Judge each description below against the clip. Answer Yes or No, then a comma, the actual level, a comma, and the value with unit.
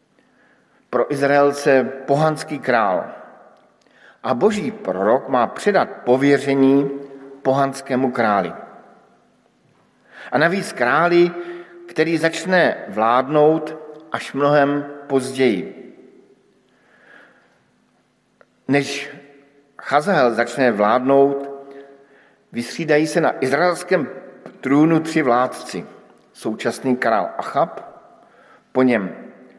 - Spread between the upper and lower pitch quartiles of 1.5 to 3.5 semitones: Yes, average, 2.9 semitones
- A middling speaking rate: No, slow, 75 wpm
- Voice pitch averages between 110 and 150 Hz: Yes, medium, 140 Hz